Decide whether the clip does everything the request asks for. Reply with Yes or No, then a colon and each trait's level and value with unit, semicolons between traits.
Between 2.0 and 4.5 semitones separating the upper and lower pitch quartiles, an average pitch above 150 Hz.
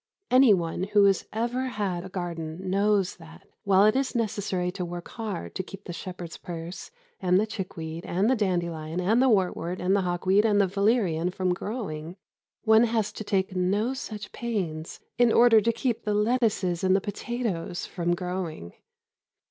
Yes: average, 3.5 semitones; high, 190 Hz